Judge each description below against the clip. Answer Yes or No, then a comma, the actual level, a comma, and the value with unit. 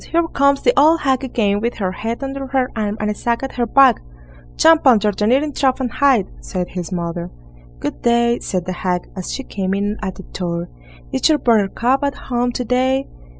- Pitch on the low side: No, high, 235 Hz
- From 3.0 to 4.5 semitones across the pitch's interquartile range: No, wide, 5.4 semitones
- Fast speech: Yes, fast, 210 wpm